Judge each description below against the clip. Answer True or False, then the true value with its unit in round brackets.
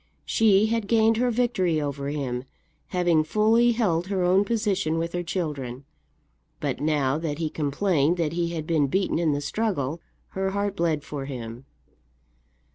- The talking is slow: False (160 wpm)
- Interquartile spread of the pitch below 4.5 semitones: False (5.5 semitones)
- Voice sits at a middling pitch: True (170 Hz)